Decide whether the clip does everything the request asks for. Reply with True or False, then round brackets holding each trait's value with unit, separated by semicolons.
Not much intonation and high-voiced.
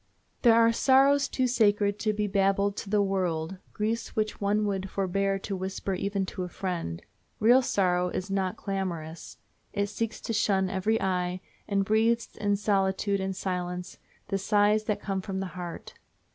True (2.0 semitones; 195 Hz)